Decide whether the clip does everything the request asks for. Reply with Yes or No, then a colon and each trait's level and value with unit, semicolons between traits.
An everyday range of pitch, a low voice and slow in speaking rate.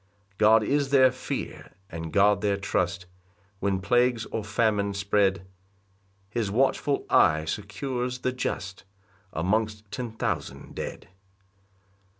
Yes: average, 3.7 semitones; low, 105 Hz; slow, 120 wpm